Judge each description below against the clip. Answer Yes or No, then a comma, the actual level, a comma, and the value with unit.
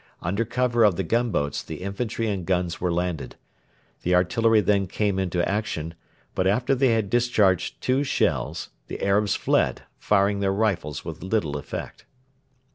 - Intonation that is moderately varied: Yes, average, 4.0 semitones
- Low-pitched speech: Yes, low, 100 Hz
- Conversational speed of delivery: Yes, average, 155 wpm